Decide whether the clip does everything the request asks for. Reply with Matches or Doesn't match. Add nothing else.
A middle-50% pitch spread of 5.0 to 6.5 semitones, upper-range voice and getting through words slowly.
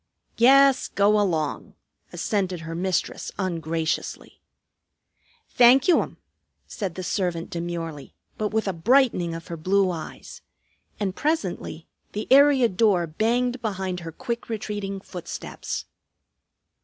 Matches